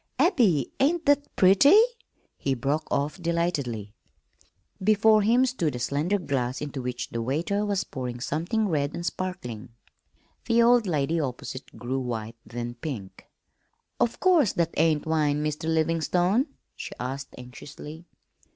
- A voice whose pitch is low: No, medium, 155 Hz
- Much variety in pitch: Yes, wide, 7.3 semitones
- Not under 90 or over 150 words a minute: Yes, slow, 135 wpm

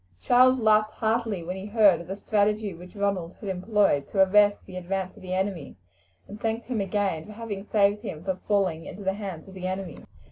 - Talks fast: Yes, fast, 210 wpm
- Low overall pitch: No, high, 200 Hz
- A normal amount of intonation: No, narrow, 2.3 semitones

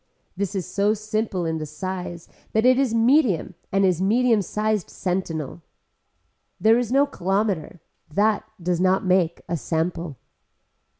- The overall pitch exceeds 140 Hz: Yes, high, 190 Hz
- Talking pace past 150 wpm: No, slow, 135 wpm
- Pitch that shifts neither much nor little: Yes, average, 3.9 semitones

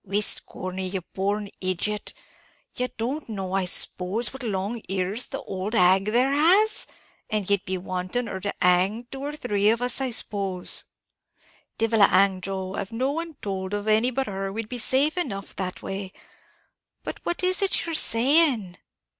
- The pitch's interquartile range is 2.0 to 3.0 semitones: No, average, 4.7 semitones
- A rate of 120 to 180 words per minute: Yes, average, 175 wpm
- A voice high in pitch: Yes, high, 210 Hz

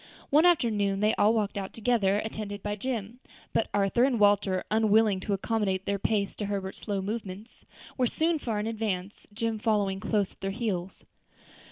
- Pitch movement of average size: No, narrow, 2.3 semitones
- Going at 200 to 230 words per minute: No, average, 175 wpm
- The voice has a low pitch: No, high, 210 Hz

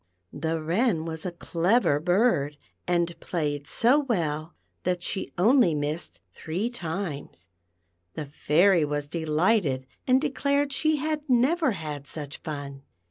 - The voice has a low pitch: No, medium, 170 Hz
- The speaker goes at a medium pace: No, slow, 130 wpm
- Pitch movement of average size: No, wide, 7.9 semitones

